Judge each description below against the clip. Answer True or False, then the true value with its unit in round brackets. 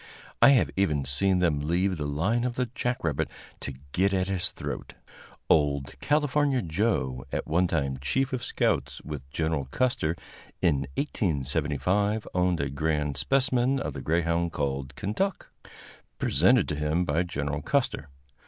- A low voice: True (85 Hz)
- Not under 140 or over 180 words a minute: True (150 wpm)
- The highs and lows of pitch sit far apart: True (6.8 semitones)